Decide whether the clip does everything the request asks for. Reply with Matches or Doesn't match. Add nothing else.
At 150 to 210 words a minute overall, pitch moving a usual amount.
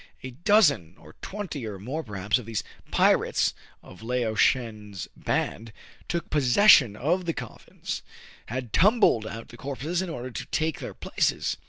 Doesn't match